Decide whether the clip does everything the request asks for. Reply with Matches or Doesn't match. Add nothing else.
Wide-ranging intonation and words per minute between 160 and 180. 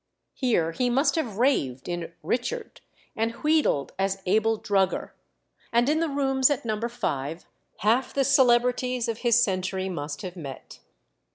Doesn't match